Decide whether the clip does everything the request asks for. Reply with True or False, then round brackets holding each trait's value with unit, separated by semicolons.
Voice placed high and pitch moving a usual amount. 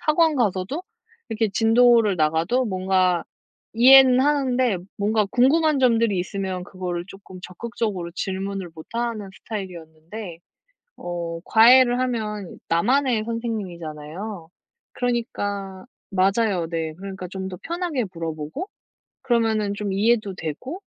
True (205 Hz; 4.7 semitones)